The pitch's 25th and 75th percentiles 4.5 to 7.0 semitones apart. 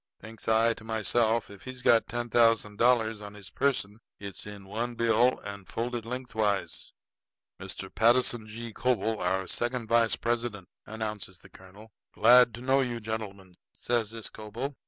No: narrow, 2.5 semitones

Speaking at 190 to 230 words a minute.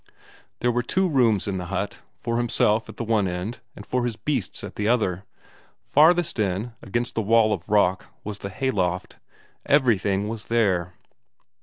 No: average, 170 wpm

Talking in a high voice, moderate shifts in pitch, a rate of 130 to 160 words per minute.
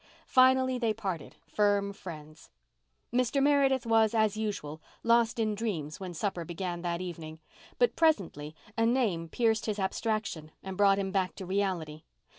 Yes: high, 200 Hz; average, 4.9 semitones; average, 150 wpm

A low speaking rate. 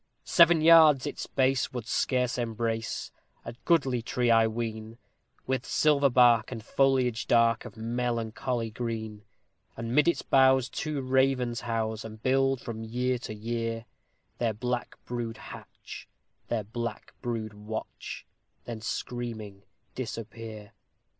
Yes: slow, 125 wpm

